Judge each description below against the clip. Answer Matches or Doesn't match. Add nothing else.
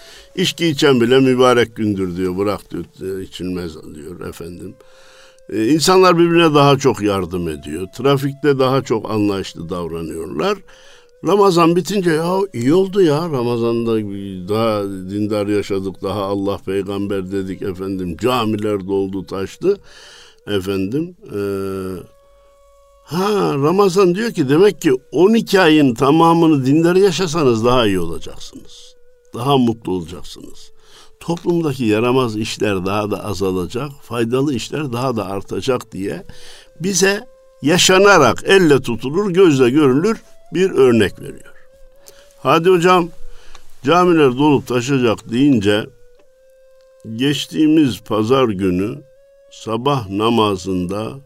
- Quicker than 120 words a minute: Doesn't match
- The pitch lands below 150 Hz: Matches